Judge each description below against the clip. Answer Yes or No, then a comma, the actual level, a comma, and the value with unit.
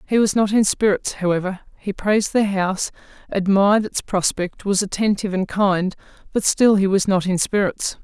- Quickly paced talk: No, average, 180 wpm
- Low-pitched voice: No, high, 195 Hz